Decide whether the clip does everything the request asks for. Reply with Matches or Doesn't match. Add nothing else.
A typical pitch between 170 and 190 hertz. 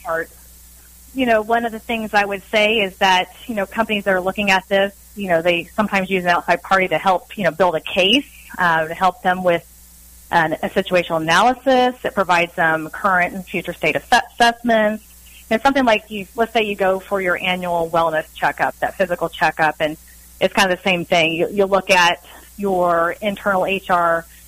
Matches